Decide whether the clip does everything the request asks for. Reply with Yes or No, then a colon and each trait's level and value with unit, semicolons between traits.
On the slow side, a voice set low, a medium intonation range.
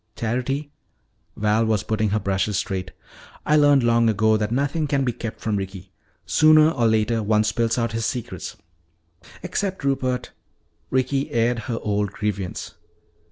No: average, 150 wpm; low, 115 Hz; average, 4.1 semitones